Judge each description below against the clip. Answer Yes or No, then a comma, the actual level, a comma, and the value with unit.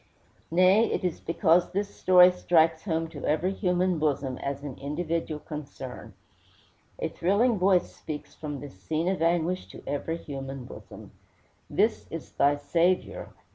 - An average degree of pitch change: Yes, average, 3.8 semitones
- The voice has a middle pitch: Yes, medium, 165 Hz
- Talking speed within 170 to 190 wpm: No, average, 145 wpm